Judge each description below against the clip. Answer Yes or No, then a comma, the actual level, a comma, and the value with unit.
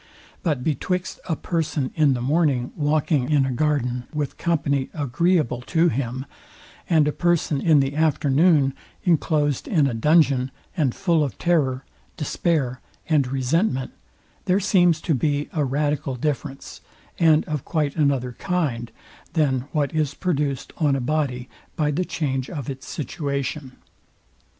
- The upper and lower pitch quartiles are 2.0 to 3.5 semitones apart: Yes, average, 3.2 semitones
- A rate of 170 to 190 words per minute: No, average, 140 wpm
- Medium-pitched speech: Yes, medium, 145 Hz